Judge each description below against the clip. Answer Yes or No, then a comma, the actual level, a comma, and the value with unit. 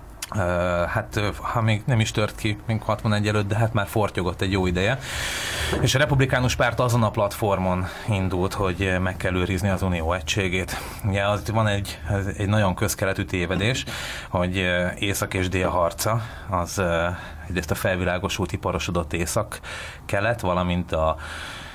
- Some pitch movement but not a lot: Yes, average, 3.1 semitones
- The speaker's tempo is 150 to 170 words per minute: Yes, fast, 155 wpm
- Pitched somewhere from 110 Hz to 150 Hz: No, very low, 95 Hz